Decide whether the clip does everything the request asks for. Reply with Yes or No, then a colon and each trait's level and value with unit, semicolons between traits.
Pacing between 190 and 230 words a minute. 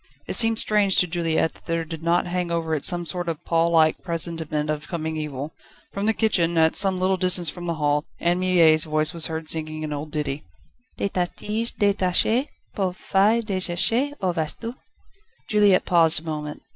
Yes: average, 200 wpm